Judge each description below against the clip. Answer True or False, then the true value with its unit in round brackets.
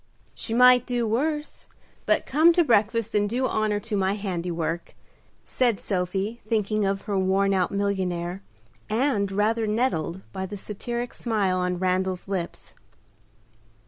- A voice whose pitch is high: True (205 Hz)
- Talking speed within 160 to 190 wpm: False (140 wpm)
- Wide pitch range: False (3.6 semitones)